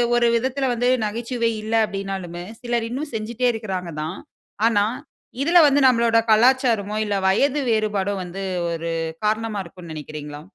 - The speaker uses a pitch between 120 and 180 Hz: No, high, 215 Hz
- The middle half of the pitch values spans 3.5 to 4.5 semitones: Yes, average, 3.9 semitones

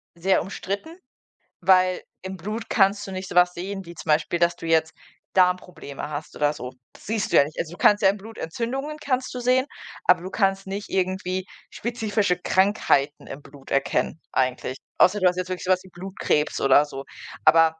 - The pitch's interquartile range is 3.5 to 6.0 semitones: Yes, average, 3.9 semitones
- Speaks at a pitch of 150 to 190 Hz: Yes, medium, 185 Hz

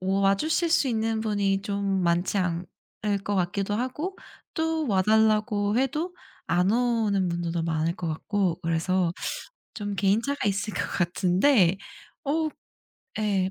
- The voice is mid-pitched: No, high, 200 Hz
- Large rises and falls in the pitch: No, average, 3.6 semitones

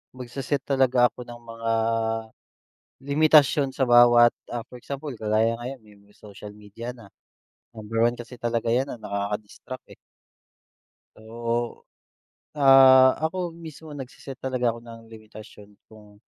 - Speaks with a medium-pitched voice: No, low, 120 Hz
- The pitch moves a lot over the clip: No, average, 3.2 semitones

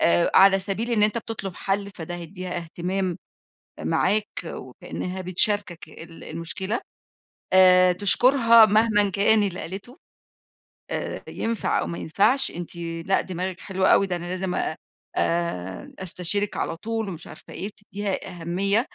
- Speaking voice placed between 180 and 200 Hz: Yes, high, 190 Hz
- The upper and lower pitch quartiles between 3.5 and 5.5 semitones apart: No, average, 2.9 semitones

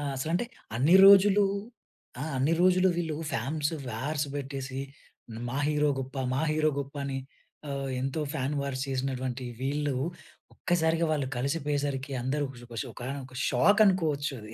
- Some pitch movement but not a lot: Yes, average, 3.0 semitones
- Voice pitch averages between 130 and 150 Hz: Yes, medium, 140 Hz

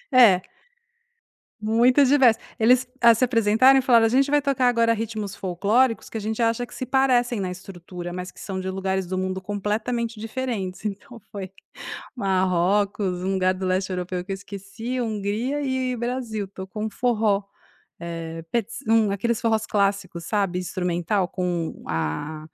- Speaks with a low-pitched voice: No, high, 210 Hz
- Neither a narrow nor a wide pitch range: Yes, average, 4.1 semitones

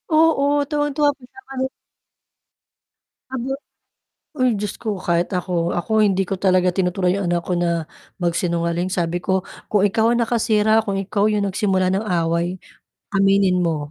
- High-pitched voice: Yes, high, 195 Hz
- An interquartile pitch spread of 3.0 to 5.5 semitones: Yes, average, 3.9 semitones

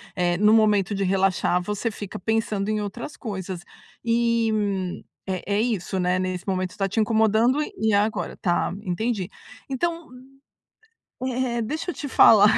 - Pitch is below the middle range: No, high, 210 Hz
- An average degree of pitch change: Yes, average, 3.3 semitones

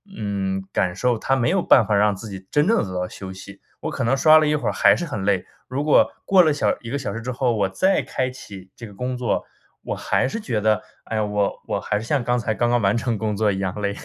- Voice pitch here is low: Yes, low, 110 Hz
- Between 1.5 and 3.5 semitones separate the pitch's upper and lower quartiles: No, average, 4.4 semitones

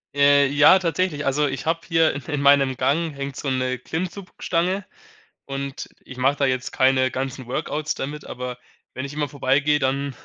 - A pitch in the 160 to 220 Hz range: No, medium, 140 Hz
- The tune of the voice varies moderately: No, narrow, 2.3 semitones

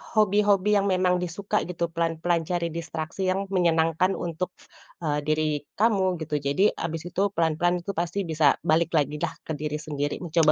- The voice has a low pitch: No, medium, 170 Hz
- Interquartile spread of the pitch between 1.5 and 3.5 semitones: Yes, average, 2.8 semitones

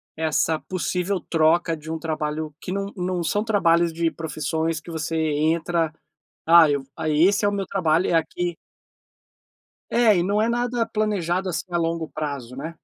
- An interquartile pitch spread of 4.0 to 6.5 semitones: No, average, 2.9 semitones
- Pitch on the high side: No, medium, 170 Hz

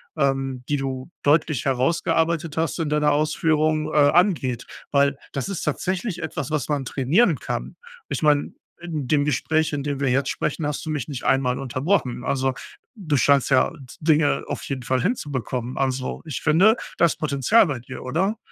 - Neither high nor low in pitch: Yes, medium, 145 Hz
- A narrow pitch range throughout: No, average, 3.0 semitones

